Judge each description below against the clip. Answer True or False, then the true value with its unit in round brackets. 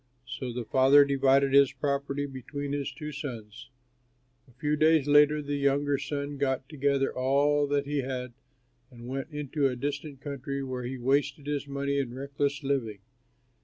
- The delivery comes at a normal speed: True (165 wpm)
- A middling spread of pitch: False (1.5 semitones)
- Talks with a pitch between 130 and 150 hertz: True (140 Hz)